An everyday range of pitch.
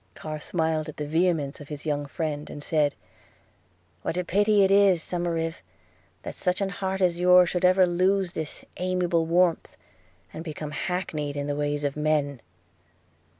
Yes: average, 3.4 semitones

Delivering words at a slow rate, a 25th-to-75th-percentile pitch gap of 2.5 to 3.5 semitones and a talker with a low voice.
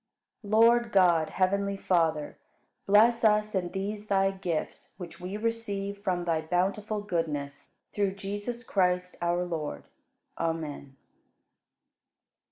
No: slow, 115 wpm; average, 3.2 semitones; high, 195 Hz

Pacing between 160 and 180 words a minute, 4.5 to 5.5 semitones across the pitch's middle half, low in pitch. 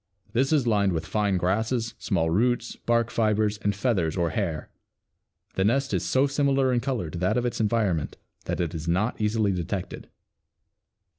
Yes: average, 170 wpm; average, 5.0 semitones; low, 105 Hz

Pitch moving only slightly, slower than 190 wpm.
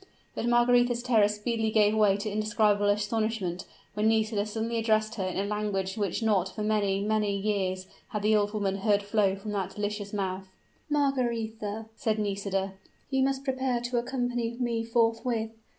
Yes: narrow, 2.2 semitones; average, 165 wpm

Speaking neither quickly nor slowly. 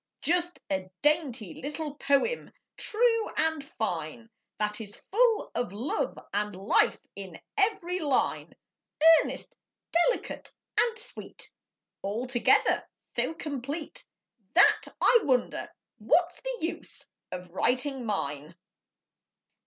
No: slow, 105 wpm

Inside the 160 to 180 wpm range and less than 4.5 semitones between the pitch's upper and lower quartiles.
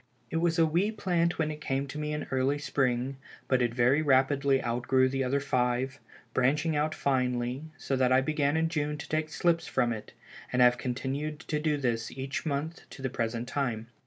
No: average, 200 wpm; average, 3.2 semitones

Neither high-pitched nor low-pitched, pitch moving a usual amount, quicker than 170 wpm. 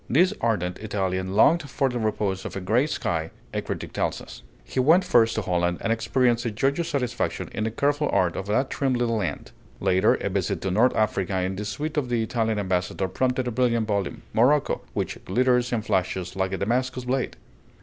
No: low, 115 Hz; average, 5.0 semitones; average, 200 wpm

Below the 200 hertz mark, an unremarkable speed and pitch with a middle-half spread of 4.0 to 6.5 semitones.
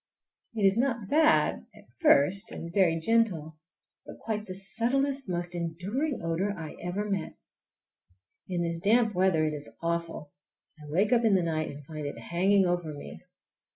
Yes: medium, 185 Hz; average, 160 wpm; average, 4.7 semitones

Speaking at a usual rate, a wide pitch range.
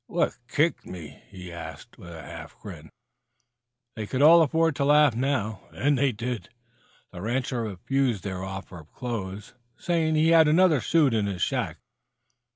Yes: average, 165 wpm; wide, 7.5 semitones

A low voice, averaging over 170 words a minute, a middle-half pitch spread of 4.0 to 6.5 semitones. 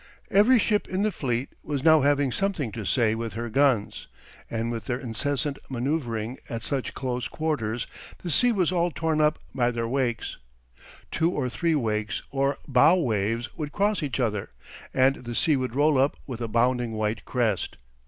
Yes: low, 130 Hz; average, 180 wpm; average, 4.8 semitones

